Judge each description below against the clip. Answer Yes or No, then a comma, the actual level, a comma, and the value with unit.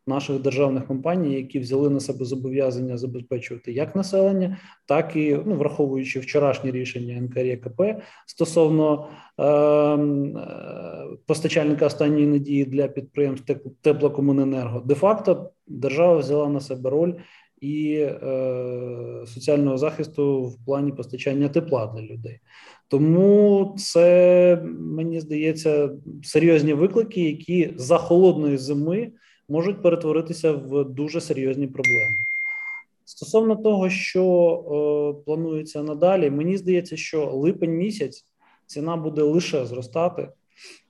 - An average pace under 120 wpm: Yes, average, 110 wpm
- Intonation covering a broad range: No, average, 3.9 semitones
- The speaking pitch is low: No, medium, 150 Hz